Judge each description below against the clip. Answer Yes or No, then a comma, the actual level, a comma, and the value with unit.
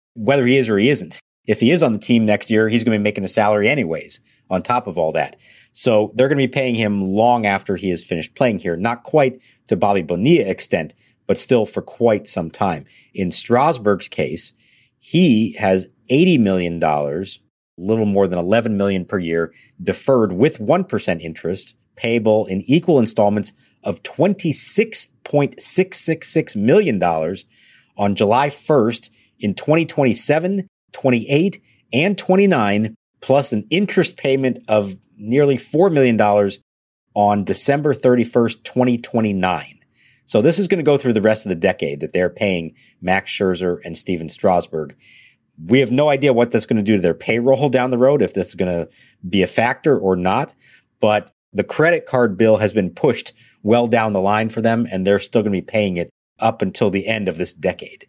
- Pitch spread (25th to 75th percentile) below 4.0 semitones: No, average, 5.3 semitones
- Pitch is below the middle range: Yes, low, 110 Hz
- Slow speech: No, average, 180 wpm